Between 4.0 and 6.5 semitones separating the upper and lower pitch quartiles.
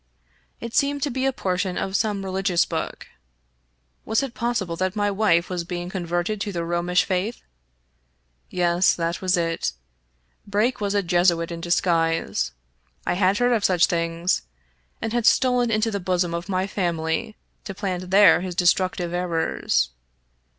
No: average, 3.1 semitones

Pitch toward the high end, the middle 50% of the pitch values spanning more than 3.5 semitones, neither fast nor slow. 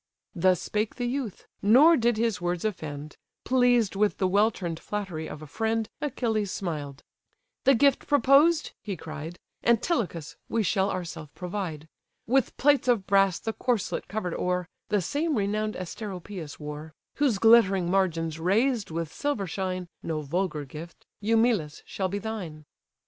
Yes: high, 195 Hz; average, 5.3 semitones; average, 150 wpm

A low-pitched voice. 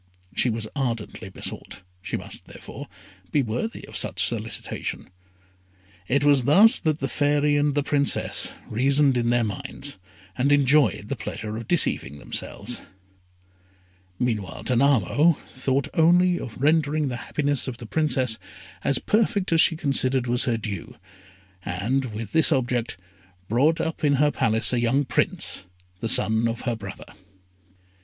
Yes: low, 130 Hz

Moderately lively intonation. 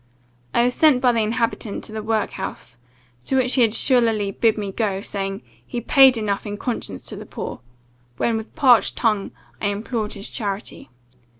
Yes: average, 3.1 semitones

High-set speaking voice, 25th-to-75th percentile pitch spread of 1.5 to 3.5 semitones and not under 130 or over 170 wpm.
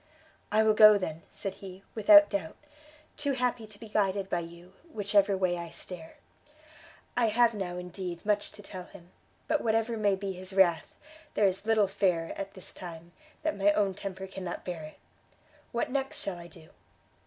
No: high, 195 Hz; average, 3.1 semitones; average, 185 wpm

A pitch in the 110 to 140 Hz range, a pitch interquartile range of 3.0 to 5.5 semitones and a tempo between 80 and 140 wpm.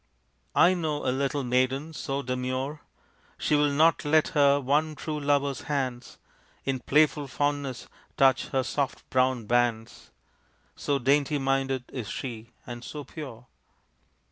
No: low, 135 Hz; narrow, 2.4 semitones; slow, 135 wpm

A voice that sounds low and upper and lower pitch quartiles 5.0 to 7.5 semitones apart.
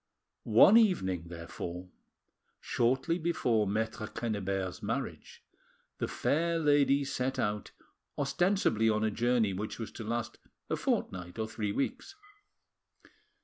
Yes: low, 115 Hz; wide, 5.6 semitones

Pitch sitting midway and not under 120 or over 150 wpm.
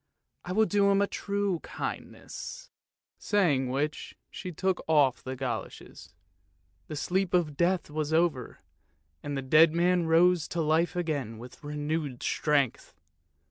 Yes: medium, 160 Hz; average, 140 wpm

